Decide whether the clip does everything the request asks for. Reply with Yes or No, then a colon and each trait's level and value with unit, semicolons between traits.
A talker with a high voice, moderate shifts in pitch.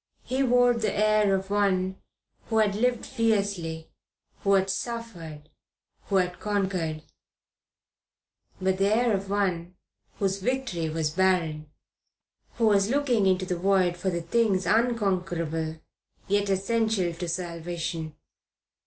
Yes: high, 195 Hz; average, 3.7 semitones